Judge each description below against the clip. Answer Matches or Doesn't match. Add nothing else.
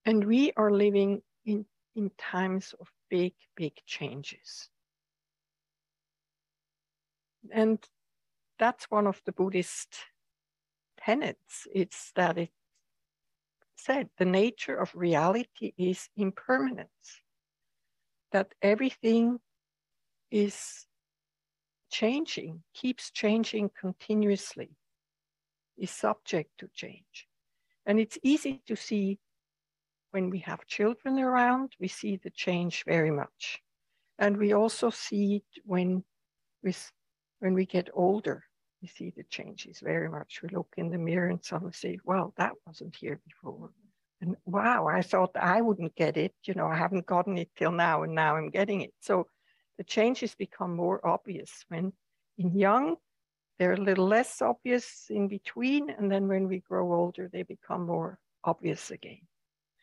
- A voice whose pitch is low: Doesn't match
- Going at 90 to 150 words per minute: Matches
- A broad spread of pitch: Doesn't match